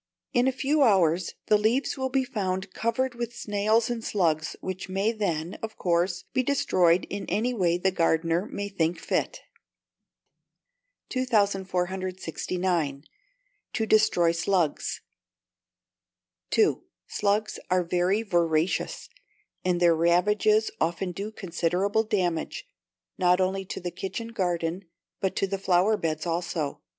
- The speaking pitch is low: No, high, 190 Hz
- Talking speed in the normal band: No, slow, 125 wpm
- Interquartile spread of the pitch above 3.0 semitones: Yes, average, 3.7 semitones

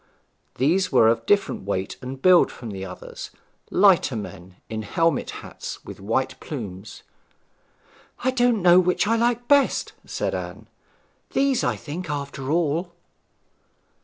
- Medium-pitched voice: Yes, medium, 150 Hz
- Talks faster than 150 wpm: No, slow, 135 wpm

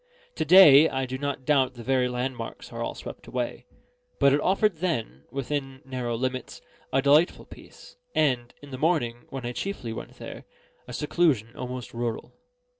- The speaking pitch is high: No, low, 130 Hz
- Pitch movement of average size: Yes, average, 3.2 semitones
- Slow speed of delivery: No, average, 170 wpm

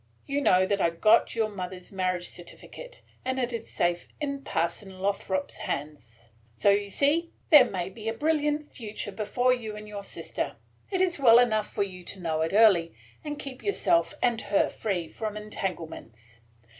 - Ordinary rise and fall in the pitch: No, wide, 5.7 semitones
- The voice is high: Yes, high, 210 Hz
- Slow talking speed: No, average, 175 wpm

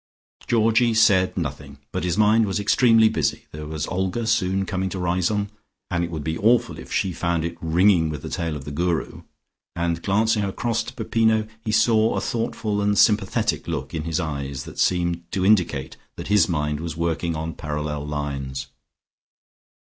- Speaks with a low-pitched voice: Yes, very low, 90 Hz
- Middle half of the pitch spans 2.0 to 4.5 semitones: No, average, 5.2 semitones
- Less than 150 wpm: No, average, 175 wpm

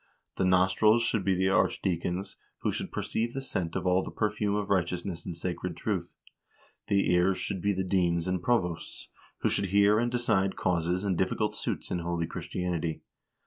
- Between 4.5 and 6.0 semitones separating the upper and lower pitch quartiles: No, narrow, 2.5 semitones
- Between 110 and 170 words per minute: No, average, 180 wpm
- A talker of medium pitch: No, very low, 95 Hz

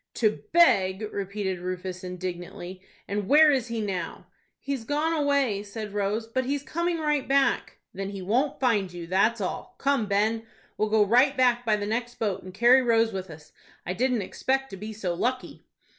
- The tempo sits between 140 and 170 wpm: No, average, 185 wpm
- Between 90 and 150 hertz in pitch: No, high, 220 Hz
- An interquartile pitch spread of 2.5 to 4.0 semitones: No, average, 5.1 semitones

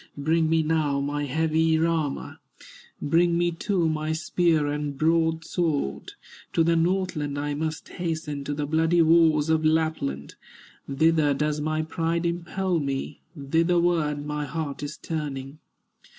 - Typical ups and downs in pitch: No, narrow, 2.0 semitones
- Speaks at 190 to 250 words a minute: No, slow, 135 wpm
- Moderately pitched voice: Yes, medium, 160 Hz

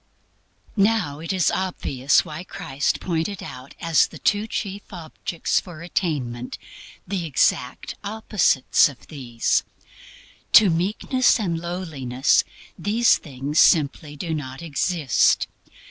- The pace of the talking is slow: Yes, slow, 115 wpm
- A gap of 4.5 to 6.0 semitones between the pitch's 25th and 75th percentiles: Yes, average, 5.1 semitones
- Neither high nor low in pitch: Yes, medium, 165 Hz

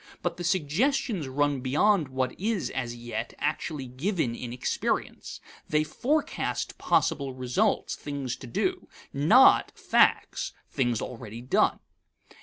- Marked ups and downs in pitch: Yes, wide, 5.7 semitones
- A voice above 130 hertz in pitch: Yes, medium, 140 Hz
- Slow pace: Yes, slow, 120 wpm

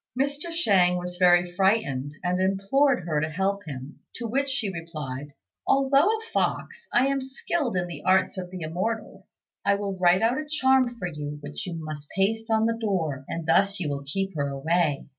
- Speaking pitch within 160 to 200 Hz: Yes, high, 190 Hz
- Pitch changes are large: Yes, wide, 5.9 semitones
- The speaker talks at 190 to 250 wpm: Yes, average, 195 wpm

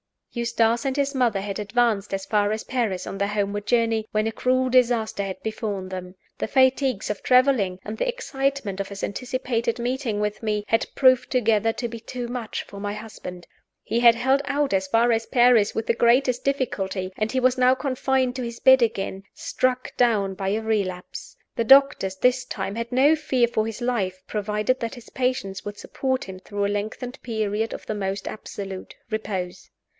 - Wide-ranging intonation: No, average, 3.8 semitones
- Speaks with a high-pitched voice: Yes, high, 225 Hz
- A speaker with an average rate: Yes, average, 190 wpm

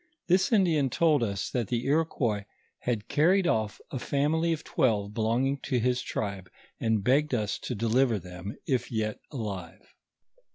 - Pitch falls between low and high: No, low, 120 Hz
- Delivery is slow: No, average, 155 wpm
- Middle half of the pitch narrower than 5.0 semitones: No, wide, 5.4 semitones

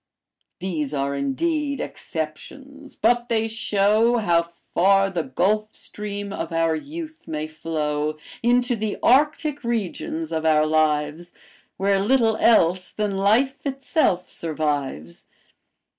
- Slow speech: Yes, slow, 115 wpm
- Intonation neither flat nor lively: No, wide, 7.2 semitones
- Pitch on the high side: Yes, high, 195 Hz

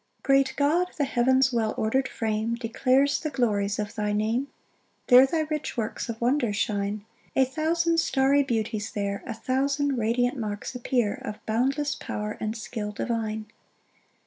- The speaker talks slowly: No, average, 155 wpm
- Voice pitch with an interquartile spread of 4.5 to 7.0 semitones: No, average, 4.1 semitones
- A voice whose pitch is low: No, high, 240 Hz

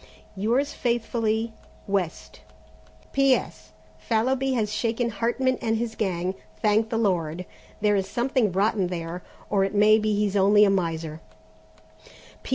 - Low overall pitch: No, high, 210 Hz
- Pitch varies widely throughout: No, average, 3.4 semitones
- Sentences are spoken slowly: Yes, slow, 130 wpm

